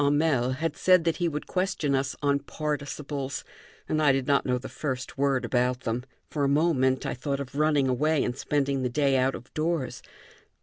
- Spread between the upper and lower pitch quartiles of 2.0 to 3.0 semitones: Yes, narrow, 2.6 semitones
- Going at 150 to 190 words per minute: No, average, 200 wpm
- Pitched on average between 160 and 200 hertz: No, medium, 140 Hz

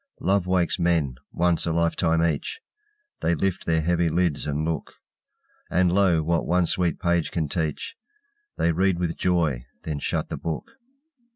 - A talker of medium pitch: No, very low, 85 Hz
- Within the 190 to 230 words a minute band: No, average, 160 wpm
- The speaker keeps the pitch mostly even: Yes, narrow, 1.7 semitones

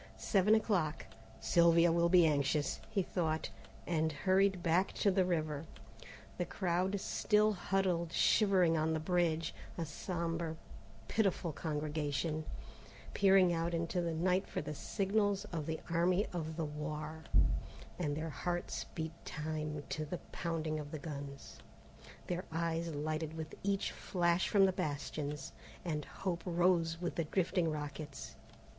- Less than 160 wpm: Yes, average, 140 wpm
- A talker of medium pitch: Yes, medium, 165 Hz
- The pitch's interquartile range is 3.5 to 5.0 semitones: No, average, 2.7 semitones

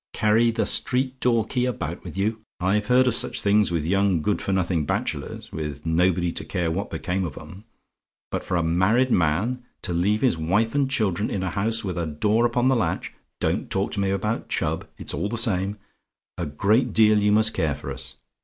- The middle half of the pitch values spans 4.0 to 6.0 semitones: Yes, average, 4.6 semitones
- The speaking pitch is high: No, low, 100 Hz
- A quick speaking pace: Yes, fast, 210 wpm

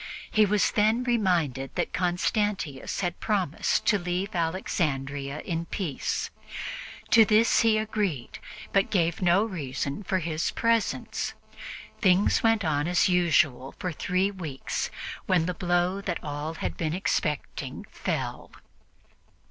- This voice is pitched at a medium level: Yes, medium, 180 Hz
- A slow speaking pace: Yes, slow, 125 wpm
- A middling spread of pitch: Yes, average, 4.6 semitones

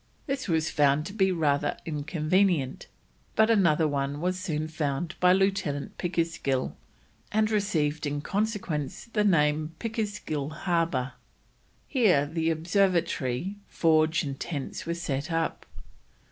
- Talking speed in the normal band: No, slow, 120 wpm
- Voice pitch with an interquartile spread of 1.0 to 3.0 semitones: No, average, 4.5 semitones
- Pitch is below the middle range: No, medium, 165 Hz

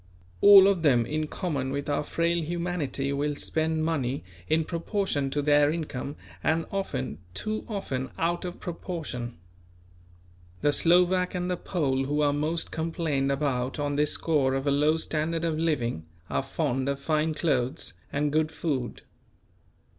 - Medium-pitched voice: Yes, medium, 150 Hz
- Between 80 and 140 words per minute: No, average, 155 wpm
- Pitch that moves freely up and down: No, average, 3.2 semitones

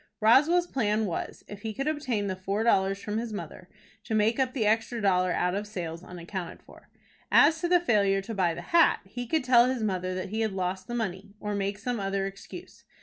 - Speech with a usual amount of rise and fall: Yes, average, 3.8 semitones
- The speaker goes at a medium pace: No, fast, 220 wpm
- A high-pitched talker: Yes, high, 210 Hz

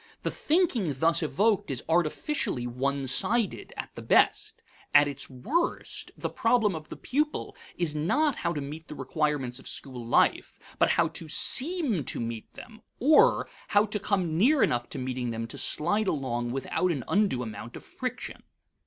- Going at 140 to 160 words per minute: No, average, 170 wpm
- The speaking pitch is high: No, medium, 160 Hz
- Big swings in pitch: Yes, wide, 8.8 semitones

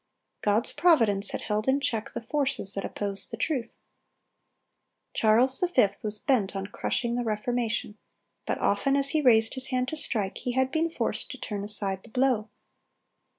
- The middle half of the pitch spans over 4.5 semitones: No, average, 4.0 semitones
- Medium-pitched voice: No, high, 230 Hz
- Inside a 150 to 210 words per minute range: Yes, average, 170 wpm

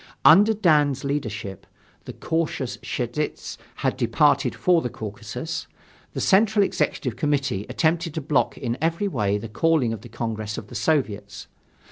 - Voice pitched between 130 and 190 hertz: Yes, low, 135 Hz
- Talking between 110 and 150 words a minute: Yes, average, 145 wpm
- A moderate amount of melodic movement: No, wide, 6.5 semitones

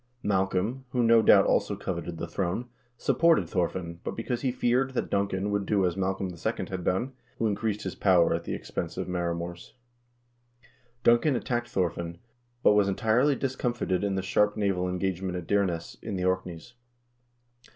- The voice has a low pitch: Yes, very low, 95 Hz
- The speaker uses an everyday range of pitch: Yes, average, 4.1 semitones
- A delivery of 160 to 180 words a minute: Yes, average, 170 wpm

